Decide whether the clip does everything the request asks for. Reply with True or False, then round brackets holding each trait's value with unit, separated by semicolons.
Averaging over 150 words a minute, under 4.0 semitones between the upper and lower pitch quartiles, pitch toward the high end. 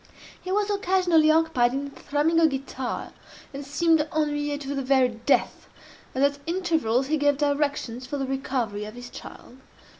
True (160 wpm; 3.3 semitones; 285 Hz)